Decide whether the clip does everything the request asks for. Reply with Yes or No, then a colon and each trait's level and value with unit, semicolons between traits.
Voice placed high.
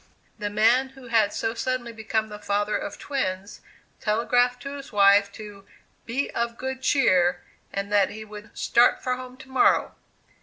Yes: high, 225 Hz